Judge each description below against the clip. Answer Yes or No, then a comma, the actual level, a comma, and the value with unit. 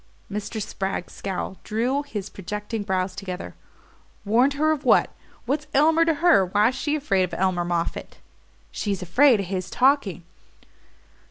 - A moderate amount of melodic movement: No, wide, 6.8 semitones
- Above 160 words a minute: No, average, 145 wpm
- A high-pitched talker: Yes, high, 210 Hz